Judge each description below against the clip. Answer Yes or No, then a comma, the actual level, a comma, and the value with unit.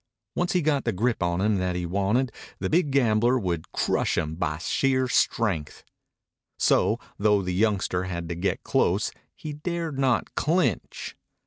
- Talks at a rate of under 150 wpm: No, average, 160 wpm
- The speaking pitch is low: Yes, low, 110 Hz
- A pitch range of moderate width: No, wide, 6.9 semitones